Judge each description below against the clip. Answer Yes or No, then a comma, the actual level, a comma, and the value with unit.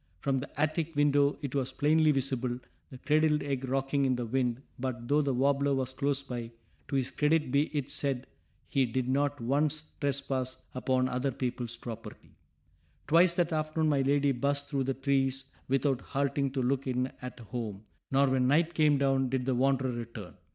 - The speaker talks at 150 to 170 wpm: No, average, 180 wpm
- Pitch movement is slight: Yes, narrow, 2.0 semitones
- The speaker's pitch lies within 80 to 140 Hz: Yes, low, 135 Hz